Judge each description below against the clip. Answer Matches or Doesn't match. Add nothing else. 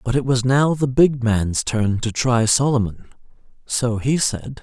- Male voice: Matches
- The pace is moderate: Matches